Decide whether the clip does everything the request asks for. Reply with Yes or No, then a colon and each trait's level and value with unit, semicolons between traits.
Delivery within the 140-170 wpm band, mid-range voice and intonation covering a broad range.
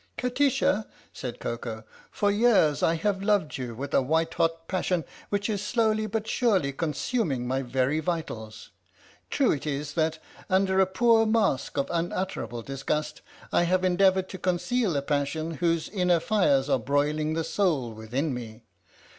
Yes: average, 165 wpm; medium, 165 Hz; wide, 6.0 semitones